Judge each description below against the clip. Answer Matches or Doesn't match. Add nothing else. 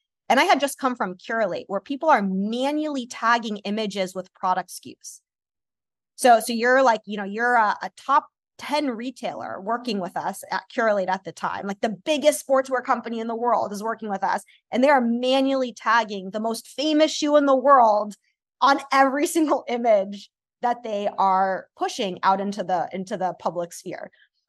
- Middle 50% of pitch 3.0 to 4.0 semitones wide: Doesn't match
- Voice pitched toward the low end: Doesn't match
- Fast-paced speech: Doesn't match